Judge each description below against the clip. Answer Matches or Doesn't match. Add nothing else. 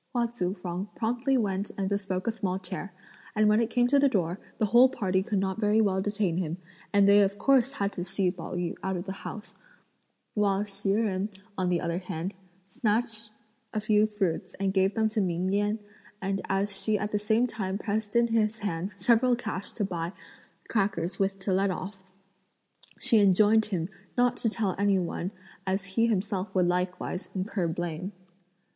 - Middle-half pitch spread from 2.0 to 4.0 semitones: Matches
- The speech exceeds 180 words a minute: Matches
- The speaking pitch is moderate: Doesn't match